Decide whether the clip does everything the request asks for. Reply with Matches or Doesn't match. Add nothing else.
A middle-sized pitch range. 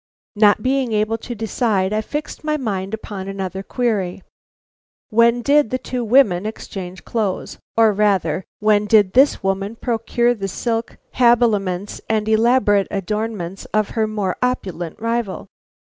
Matches